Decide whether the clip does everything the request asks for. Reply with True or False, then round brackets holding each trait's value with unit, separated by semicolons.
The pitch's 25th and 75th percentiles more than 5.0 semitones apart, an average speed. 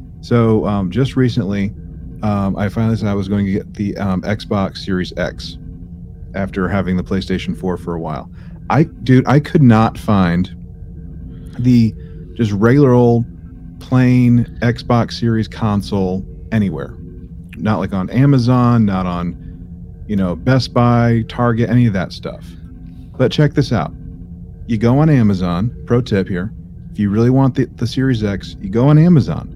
True (5.4 semitones; 160 wpm)